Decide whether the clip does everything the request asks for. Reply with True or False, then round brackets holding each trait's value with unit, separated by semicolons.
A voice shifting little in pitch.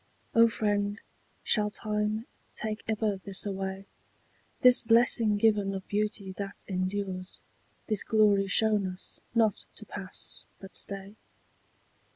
True (1.8 semitones)